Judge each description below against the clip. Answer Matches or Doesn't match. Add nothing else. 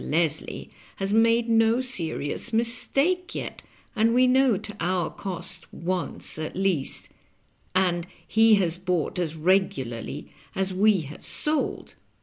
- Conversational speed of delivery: Doesn't match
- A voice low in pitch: Doesn't match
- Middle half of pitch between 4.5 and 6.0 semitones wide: Matches